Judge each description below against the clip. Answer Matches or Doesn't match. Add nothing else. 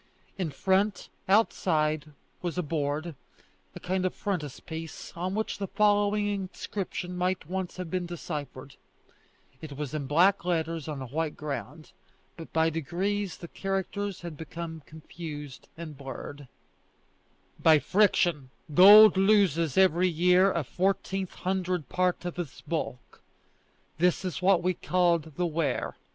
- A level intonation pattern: Doesn't match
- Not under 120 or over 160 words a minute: Matches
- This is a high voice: Doesn't match